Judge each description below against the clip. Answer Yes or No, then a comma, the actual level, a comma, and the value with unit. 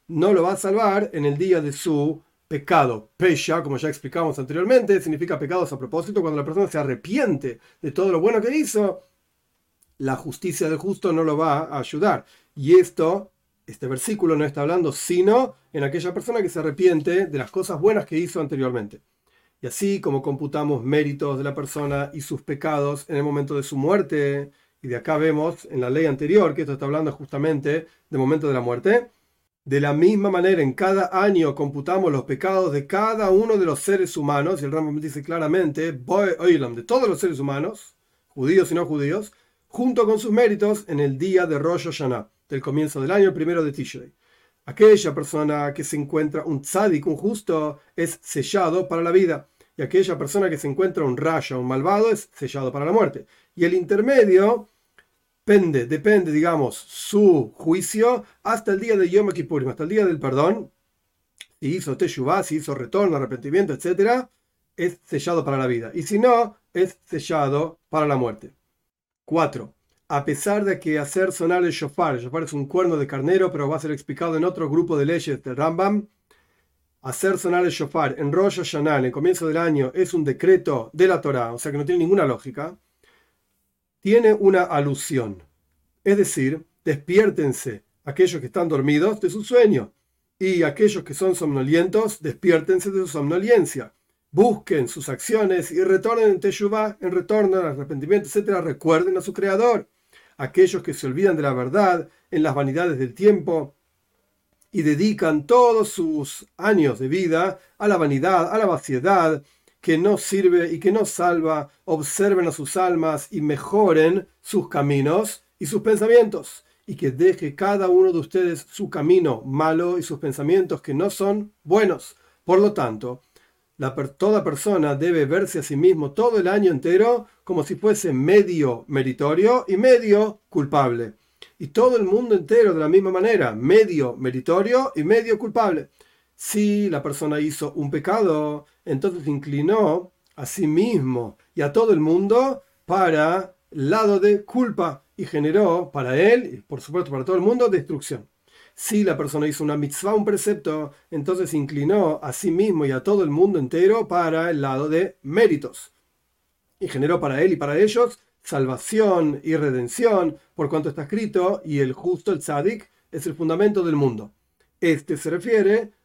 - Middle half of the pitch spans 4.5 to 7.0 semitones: Yes, average, 5.1 semitones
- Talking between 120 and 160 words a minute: No, average, 175 wpm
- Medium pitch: Yes, medium, 165 Hz